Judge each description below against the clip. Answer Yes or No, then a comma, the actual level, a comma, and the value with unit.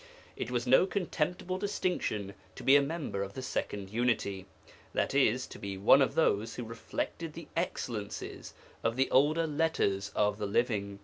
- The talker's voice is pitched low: Yes, low, 125 Hz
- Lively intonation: Yes, wide, 7.4 semitones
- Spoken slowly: No, average, 165 wpm